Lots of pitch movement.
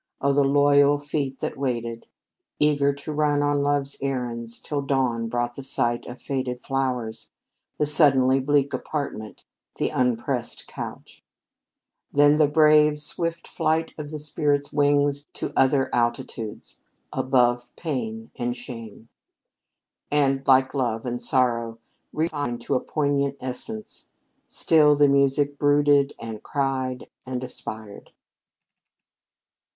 No: average, 2.9 semitones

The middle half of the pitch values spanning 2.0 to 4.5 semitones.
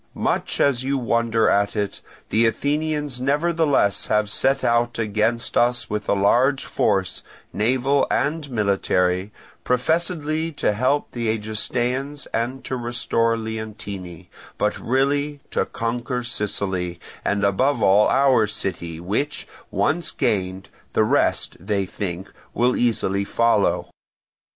No: average, 4.9 semitones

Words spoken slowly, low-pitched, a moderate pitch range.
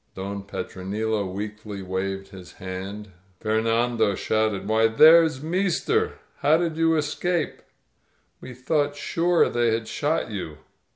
No: slow, 120 wpm; low, 110 Hz; wide, 7.5 semitones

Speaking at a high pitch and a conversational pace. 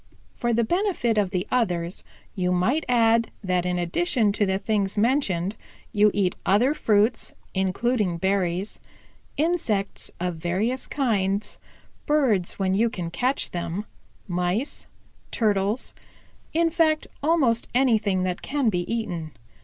No: high, 210 Hz; slow, 130 wpm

